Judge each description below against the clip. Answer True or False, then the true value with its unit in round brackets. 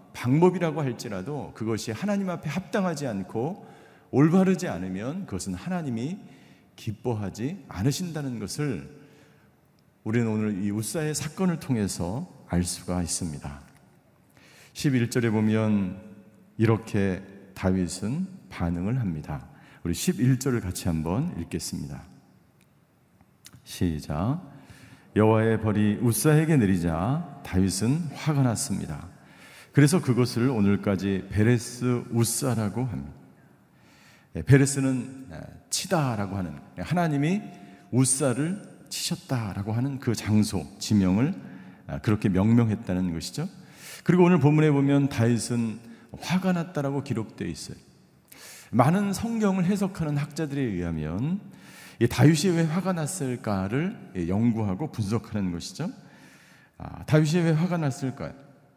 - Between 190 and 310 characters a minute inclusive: True (265 characters per minute)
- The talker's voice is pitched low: True (120 Hz)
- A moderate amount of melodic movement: False (7.5 semitones)